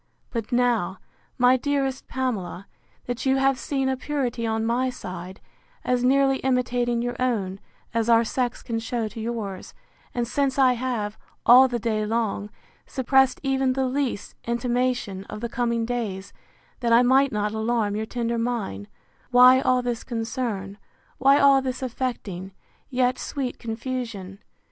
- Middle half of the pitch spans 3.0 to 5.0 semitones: No, narrow, 2.6 semitones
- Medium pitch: No, high, 240 Hz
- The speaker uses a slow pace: No, average, 150 wpm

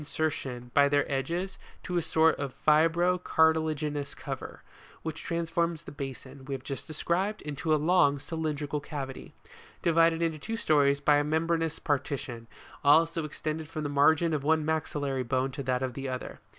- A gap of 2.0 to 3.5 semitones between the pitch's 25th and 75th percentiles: Yes, narrow, 2.6 semitones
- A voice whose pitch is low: No, medium, 150 Hz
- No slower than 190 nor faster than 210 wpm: No, average, 170 wpm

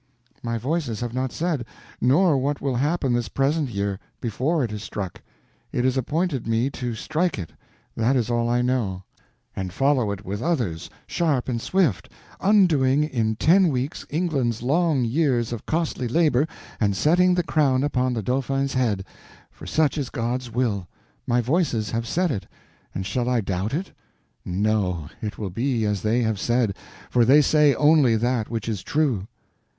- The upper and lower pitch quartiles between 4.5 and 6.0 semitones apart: Yes, average, 4.8 semitones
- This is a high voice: No, low, 125 Hz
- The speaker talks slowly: No, average, 170 wpm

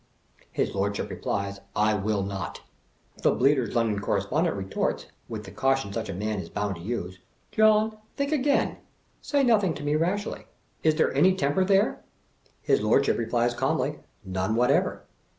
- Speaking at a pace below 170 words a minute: Yes, average, 160 wpm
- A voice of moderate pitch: No, low, 120 Hz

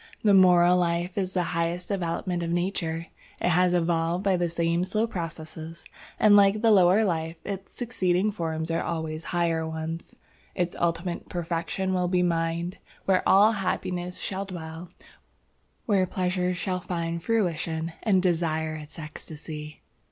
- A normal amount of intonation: No, narrow, 2.1 semitones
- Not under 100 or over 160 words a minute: Yes, average, 145 wpm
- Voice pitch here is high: No, medium, 175 Hz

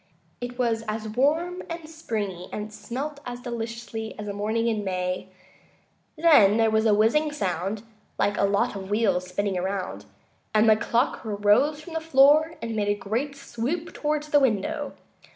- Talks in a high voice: Yes, high, 225 Hz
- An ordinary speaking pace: Yes, average, 170 wpm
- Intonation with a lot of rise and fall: Yes, wide, 5.9 semitones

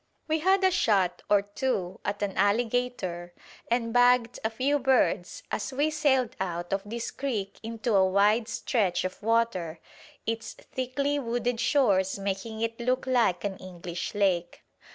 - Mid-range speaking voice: No, high, 225 Hz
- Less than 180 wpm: Yes, average, 155 wpm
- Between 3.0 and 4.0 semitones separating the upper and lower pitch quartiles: No, average, 4.6 semitones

